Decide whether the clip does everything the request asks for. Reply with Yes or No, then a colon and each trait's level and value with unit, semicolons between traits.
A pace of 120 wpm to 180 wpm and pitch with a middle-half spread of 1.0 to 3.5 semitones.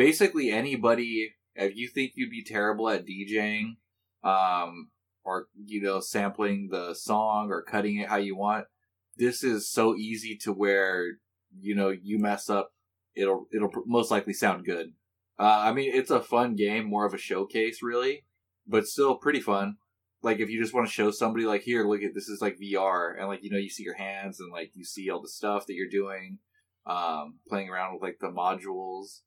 No: average, 200 wpm; narrow, 2.5 semitones